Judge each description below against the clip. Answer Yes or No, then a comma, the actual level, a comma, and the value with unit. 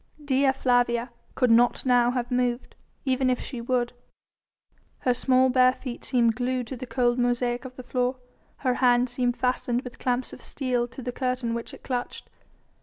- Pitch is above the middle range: Yes, very high, 250 Hz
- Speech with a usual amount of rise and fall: No, narrow, 0.9 semitones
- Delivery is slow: No, average, 180 wpm